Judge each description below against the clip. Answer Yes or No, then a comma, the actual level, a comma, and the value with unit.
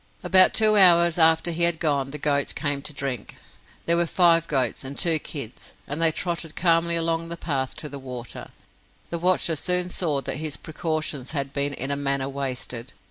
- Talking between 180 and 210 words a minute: Yes, average, 190 wpm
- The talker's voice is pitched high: No, medium, 155 Hz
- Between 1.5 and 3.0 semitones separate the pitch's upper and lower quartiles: No, average, 3.5 semitones